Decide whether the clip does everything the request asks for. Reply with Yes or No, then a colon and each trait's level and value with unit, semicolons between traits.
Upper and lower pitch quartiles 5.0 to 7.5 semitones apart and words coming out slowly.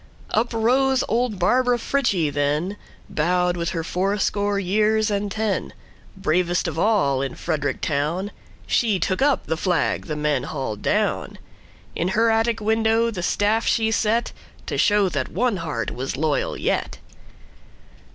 Yes: wide, 5.6 semitones; slow, 130 wpm